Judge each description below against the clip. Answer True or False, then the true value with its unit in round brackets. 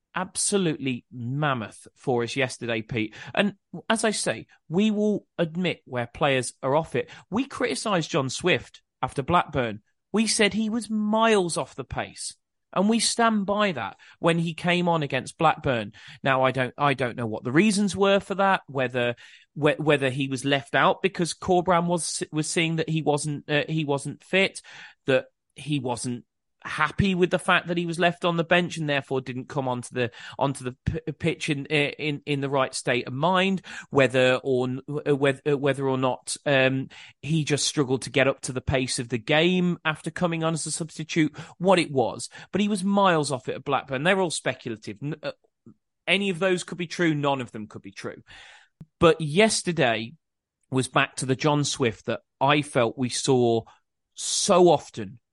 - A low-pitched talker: False (150 Hz)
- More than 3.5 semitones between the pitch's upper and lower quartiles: True (5.1 semitones)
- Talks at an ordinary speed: True (190 wpm)